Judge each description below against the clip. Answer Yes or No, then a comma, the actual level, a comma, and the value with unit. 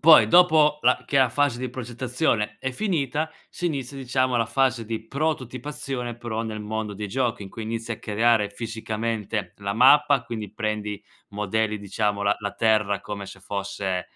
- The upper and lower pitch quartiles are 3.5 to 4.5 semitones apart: Yes, average, 3.8 semitones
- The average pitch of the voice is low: Yes, low, 115 Hz